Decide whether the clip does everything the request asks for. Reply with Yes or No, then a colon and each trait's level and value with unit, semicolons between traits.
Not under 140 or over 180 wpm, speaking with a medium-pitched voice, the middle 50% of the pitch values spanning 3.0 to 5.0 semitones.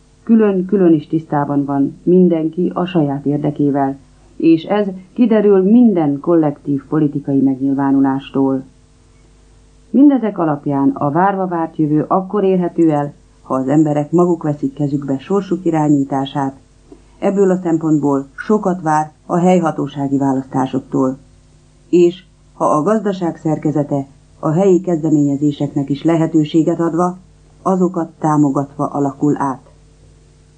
No: average, 110 wpm; medium, 150 Hz; average, 3.8 semitones